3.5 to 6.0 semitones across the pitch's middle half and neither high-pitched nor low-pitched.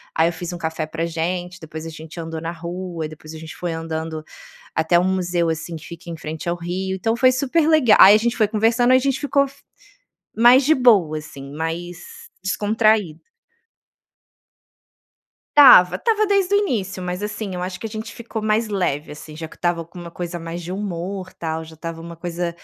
Yes: average, 5.0 semitones; medium, 175 Hz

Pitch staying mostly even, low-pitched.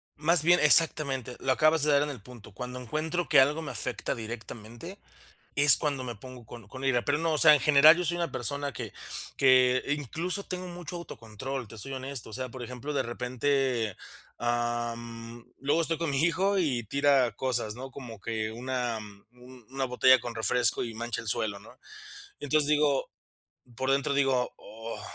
No: average, 3.8 semitones; low, 130 Hz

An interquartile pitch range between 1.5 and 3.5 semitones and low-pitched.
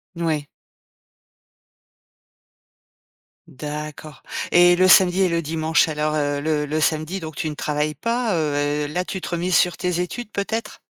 No: average, 2.9 semitones; medium, 160 Hz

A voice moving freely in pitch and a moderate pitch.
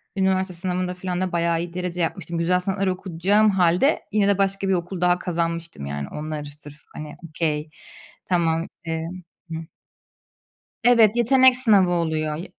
No: average, 2.7 semitones; medium, 180 Hz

